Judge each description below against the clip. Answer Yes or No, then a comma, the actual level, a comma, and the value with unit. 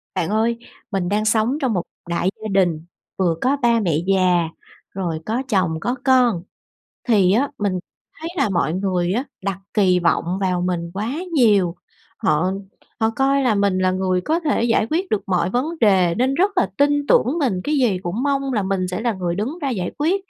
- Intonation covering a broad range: Yes, wide, 5.7 semitones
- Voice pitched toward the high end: Yes, high, 205 Hz